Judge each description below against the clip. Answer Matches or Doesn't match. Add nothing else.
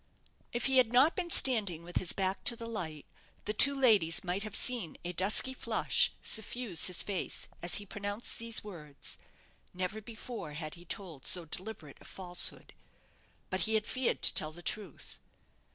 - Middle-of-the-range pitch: Doesn't match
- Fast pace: Doesn't match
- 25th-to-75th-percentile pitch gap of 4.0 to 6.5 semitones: Matches